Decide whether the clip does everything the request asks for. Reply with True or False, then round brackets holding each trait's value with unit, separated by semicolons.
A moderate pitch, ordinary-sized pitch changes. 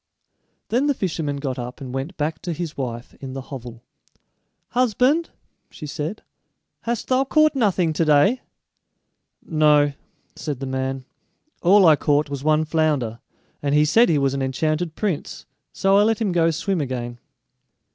False (155 Hz; 6.1 semitones)